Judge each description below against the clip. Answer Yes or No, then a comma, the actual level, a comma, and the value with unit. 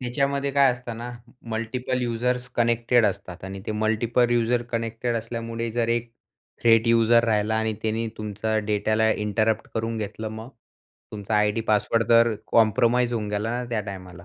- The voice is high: No, low, 115 Hz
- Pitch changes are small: Yes, narrow, 1.7 semitones